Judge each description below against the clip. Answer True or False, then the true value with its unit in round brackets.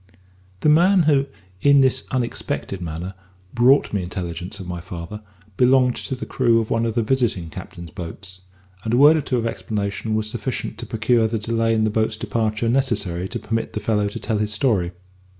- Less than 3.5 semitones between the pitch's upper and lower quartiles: False (4.1 semitones)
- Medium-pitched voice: False (110 Hz)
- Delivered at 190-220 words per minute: True (195 wpm)